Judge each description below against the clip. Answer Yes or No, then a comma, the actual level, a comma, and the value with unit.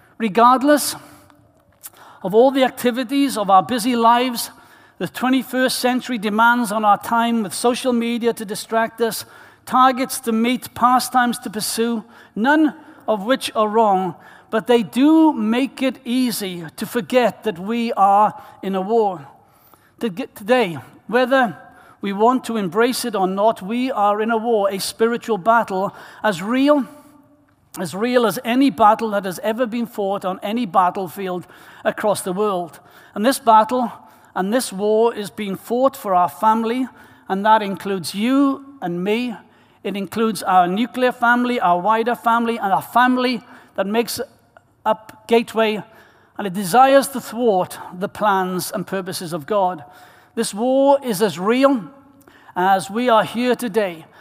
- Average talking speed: Yes, average, 150 wpm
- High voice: Yes, high, 230 Hz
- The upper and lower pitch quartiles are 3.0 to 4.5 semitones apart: Yes, average, 3.6 semitones